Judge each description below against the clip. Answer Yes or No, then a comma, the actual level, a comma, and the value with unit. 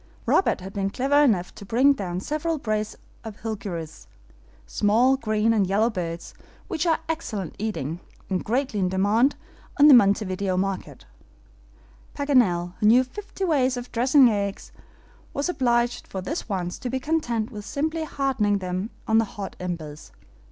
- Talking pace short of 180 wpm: Yes, average, 155 wpm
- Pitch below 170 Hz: No, high, 220 Hz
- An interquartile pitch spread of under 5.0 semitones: No, wide, 5.5 semitones